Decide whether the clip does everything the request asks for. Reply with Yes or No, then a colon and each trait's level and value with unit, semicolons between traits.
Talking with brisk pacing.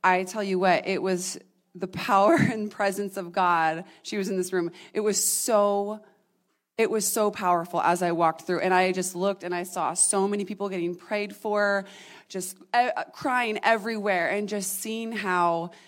No: average, 180 wpm